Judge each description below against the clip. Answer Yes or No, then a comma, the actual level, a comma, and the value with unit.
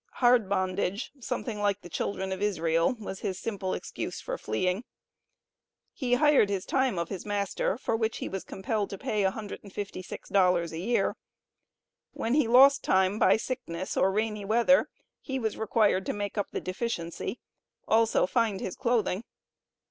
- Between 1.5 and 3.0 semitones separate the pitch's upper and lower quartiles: No, average, 3.5 semitones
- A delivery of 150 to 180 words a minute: Yes, average, 155 wpm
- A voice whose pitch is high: Yes, high, 205 Hz